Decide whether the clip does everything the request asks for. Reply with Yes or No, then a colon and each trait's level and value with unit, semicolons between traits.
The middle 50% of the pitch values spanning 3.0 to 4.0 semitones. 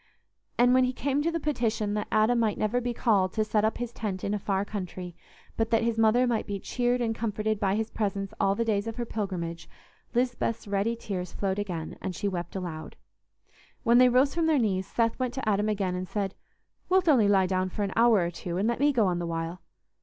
Yes: average, 3.7 semitones